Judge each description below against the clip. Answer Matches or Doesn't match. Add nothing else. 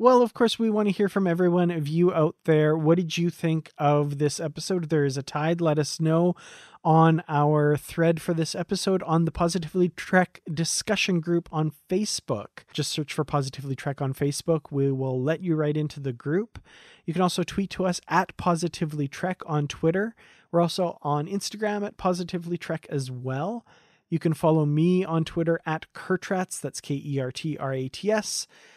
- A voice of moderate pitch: Matches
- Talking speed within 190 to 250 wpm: Matches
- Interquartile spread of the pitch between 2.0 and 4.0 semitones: Matches